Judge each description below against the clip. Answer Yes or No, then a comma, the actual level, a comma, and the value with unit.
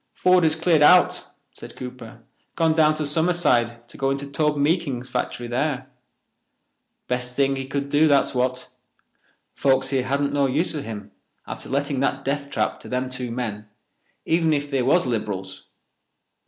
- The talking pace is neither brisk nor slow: Yes, average, 160 wpm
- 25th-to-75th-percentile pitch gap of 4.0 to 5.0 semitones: No, average, 3.1 semitones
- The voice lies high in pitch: No, low, 135 Hz